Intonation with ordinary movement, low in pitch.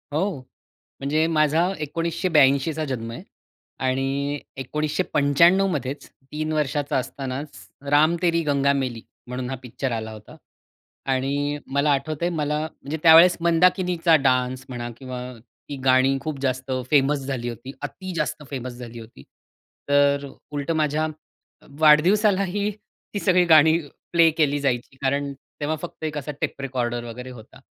No: average, 3.3 semitones; medium, 145 Hz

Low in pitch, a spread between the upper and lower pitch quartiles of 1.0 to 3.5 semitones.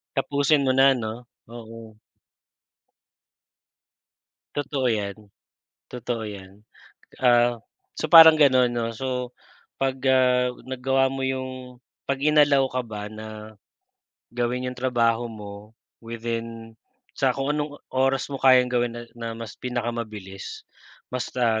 Yes: low, 125 Hz; narrow, 2.6 semitones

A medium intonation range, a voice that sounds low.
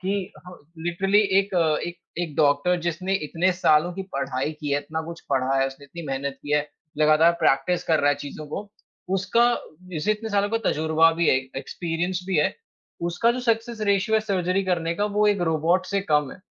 No: average, 4.2 semitones; medium, 170 Hz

